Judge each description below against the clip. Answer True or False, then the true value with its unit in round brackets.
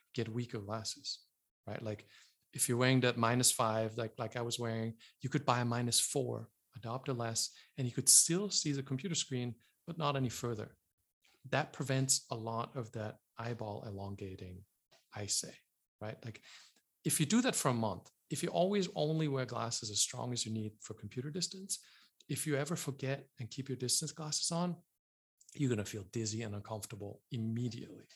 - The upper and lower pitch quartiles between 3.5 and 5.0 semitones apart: True (4.0 semitones)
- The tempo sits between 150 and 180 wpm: False (190 wpm)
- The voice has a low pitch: True (120 Hz)